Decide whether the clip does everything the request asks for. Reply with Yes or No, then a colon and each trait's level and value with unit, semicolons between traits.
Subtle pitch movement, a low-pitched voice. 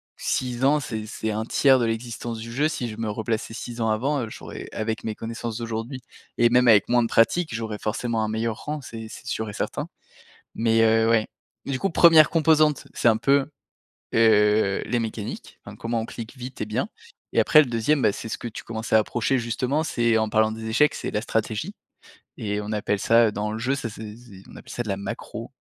Yes: narrow, 2.2 semitones; low, 115 Hz